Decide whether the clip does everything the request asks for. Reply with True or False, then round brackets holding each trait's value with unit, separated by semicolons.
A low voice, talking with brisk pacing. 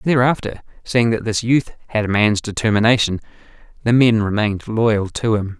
False (110 Hz; 160 wpm)